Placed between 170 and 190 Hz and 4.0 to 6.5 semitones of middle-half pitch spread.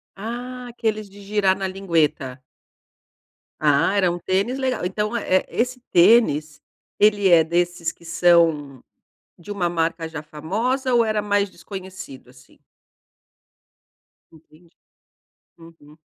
Yes: medium, 185 Hz; average, 4.4 semitones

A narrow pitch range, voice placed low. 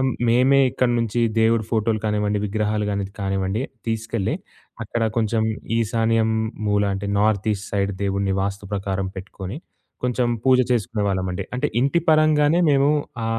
No: average, 3.1 semitones; low, 110 Hz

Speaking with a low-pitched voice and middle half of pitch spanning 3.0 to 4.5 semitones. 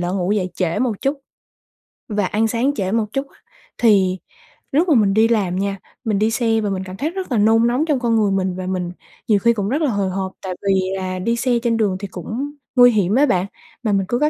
No: high, 215 Hz; average, 4.0 semitones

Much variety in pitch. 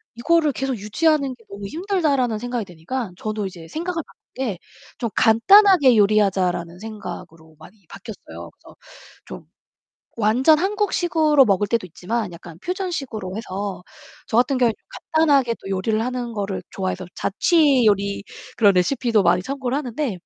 Yes: wide, 5.9 semitones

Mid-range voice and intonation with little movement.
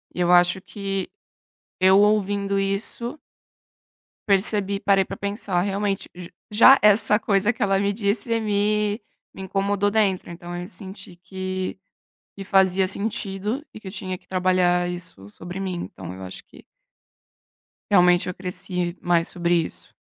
No: high, 195 Hz; narrow, 2.3 semitones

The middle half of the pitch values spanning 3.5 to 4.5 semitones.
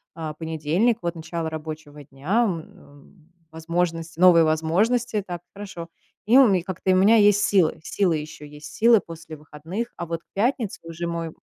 Yes: average, 3.9 semitones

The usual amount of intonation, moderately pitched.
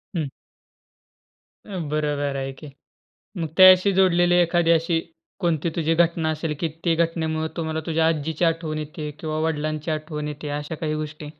No: narrow, 1.6 semitones; medium, 160 Hz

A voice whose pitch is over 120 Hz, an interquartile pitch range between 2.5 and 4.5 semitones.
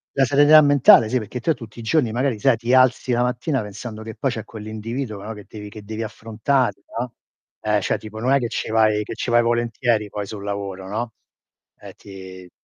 No: low, 115 Hz; average, 2.8 semitones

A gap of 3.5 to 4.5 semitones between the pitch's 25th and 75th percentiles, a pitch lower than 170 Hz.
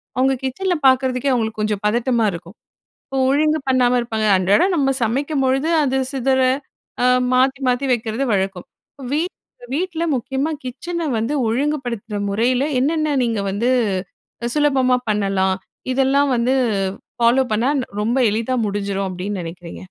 No: average, 4.2 semitones; very high, 250 Hz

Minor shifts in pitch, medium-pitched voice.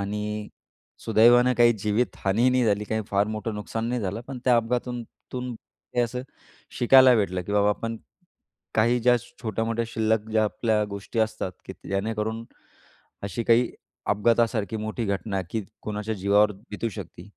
No: narrow, 2.3 semitones; low, 110 Hz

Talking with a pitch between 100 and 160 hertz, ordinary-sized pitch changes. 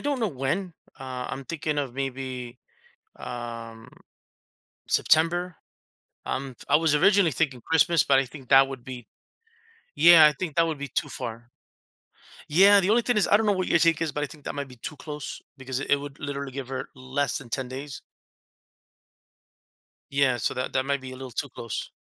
Yes: medium, 140 Hz; average, 3.9 semitones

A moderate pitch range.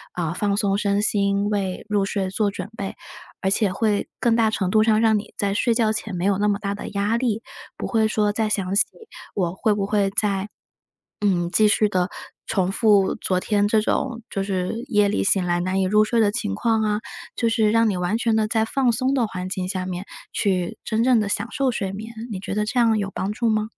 No: narrow, 2.2 semitones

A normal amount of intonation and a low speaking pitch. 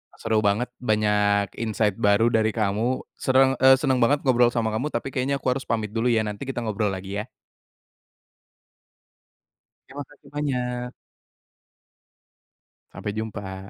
Yes: average, 3.5 semitones; low, 115 Hz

